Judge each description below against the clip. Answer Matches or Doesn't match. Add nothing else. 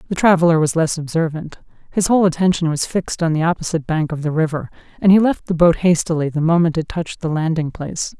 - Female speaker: Matches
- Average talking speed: Doesn't match